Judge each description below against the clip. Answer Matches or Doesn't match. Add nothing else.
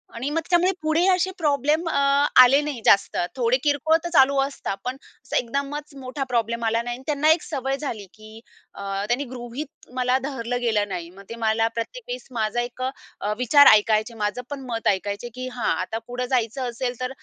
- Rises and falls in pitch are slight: Doesn't match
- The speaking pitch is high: Matches